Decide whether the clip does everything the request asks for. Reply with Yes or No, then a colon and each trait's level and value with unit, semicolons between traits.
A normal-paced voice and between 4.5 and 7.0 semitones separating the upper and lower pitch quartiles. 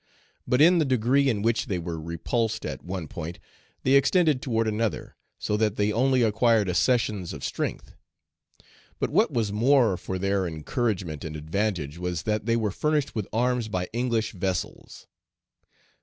Yes: average, 160 wpm; average, 5.0 semitones